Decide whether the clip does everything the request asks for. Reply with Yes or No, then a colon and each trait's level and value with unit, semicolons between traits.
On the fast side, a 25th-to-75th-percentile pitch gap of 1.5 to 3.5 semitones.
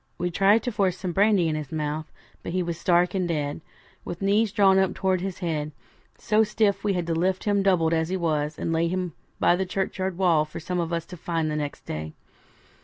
Yes: fast, 225 wpm; average, 2.9 semitones